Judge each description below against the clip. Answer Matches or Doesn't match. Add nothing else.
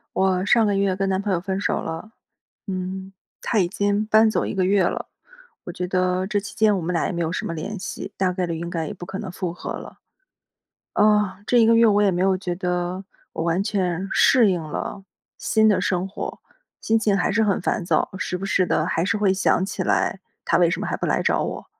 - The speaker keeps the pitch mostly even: Matches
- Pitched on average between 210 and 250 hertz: Doesn't match